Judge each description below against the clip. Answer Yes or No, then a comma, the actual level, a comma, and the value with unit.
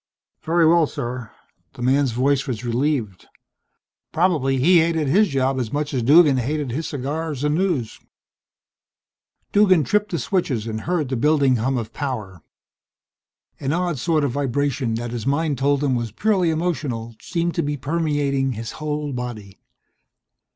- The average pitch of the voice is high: No, medium, 140 Hz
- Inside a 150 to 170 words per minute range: Yes, average, 155 wpm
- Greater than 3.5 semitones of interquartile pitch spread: Yes, average, 4.5 semitones